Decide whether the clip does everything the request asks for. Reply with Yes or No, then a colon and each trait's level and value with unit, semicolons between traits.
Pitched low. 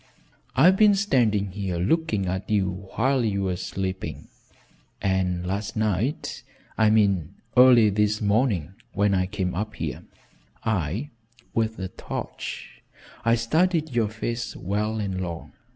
Yes: low, 105 Hz